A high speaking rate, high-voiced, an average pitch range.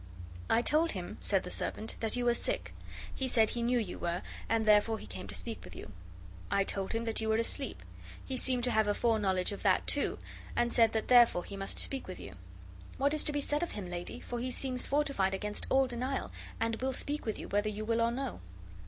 Yes: fast, 235 wpm; high, 230 Hz; average, 3.5 semitones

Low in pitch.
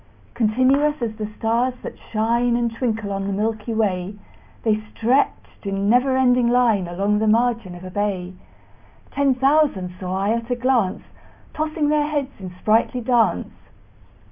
No: high, 230 Hz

